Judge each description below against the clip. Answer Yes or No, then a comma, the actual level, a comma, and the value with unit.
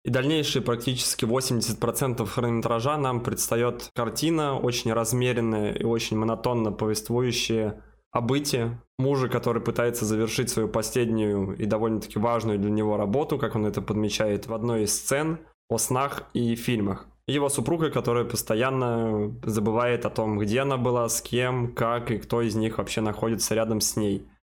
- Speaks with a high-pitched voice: No, low, 115 Hz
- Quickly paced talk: No, average, 150 wpm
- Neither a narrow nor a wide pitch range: No, narrow, 2.2 semitones